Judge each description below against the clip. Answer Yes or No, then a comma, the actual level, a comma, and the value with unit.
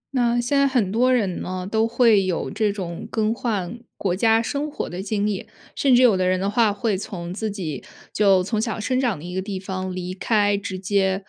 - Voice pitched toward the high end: Yes, high, 205 Hz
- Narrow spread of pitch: No, average, 3.5 semitones